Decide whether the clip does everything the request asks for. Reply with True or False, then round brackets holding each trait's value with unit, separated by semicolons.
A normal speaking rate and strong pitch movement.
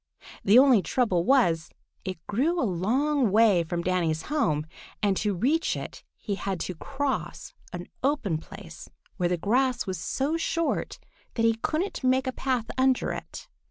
True (160 wpm; 6.9 semitones)